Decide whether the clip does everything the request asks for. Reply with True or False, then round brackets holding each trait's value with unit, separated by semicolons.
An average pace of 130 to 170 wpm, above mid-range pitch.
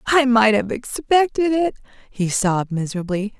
True (140 wpm; 235 Hz)